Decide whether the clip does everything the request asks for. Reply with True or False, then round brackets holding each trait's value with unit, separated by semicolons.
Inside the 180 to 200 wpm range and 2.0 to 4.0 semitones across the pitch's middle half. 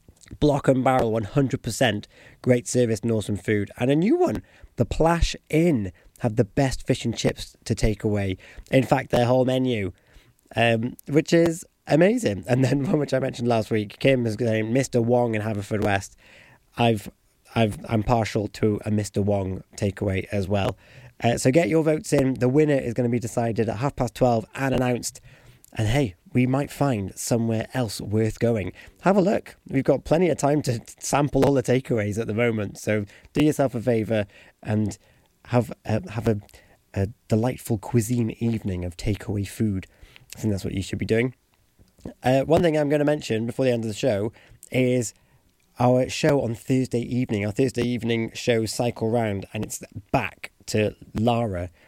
True (185 wpm; 3.4 semitones)